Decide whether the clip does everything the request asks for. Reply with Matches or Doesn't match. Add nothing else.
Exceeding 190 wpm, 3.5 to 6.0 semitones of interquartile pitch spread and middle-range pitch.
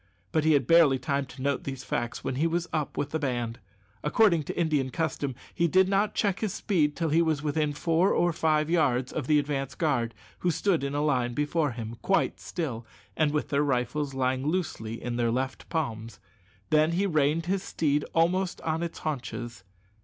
Matches